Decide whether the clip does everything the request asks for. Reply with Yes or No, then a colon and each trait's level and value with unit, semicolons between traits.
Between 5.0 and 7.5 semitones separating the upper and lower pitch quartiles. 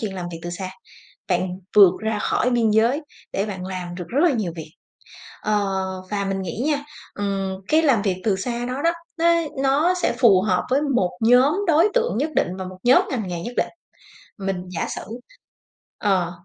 Yes: wide, 5.6 semitones